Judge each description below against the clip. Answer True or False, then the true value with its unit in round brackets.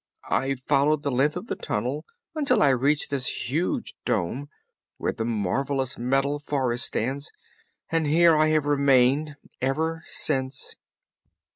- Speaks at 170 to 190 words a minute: False (135 wpm)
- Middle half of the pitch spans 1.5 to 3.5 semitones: True (2.5 semitones)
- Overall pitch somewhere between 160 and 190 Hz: False (140 Hz)